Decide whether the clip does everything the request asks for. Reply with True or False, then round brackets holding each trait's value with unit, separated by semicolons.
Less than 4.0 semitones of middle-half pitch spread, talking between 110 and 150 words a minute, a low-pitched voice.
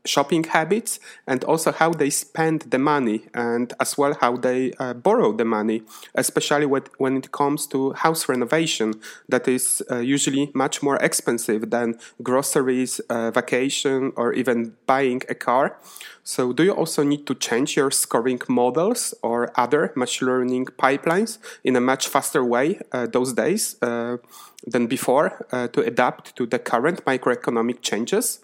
False (3.1 semitones; 160 wpm; 130 Hz)